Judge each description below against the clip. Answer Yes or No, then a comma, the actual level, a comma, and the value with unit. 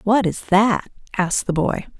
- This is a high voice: Yes, high, 200 Hz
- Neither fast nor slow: Yes, average, 180 wpm